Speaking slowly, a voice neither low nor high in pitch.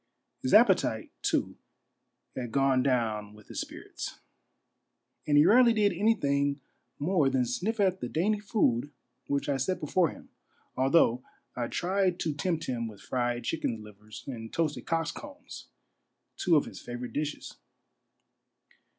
No: average, 145 wpm; medium, 145 Hz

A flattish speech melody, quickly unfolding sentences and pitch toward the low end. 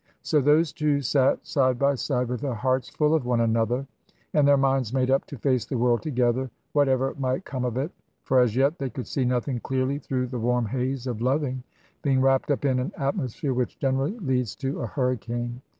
Yes: narrow, 1.9 semitones; fast, 210 wpm; low, 130 Hz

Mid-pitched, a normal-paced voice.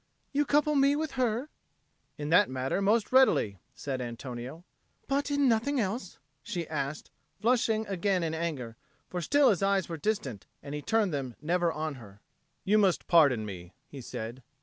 Yes: medium, 175 Hz; average, 170 wpm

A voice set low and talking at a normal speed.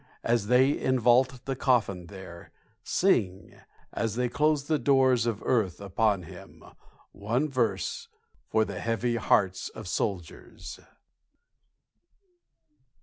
No: low, 115 Hz; slow, 110 wpm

